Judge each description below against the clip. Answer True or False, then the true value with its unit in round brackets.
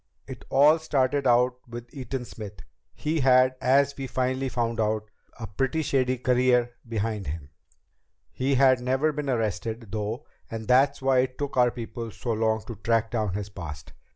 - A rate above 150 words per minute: True (170 wpm)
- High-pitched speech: False (125 Hz)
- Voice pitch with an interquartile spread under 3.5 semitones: True (3.1 semitones)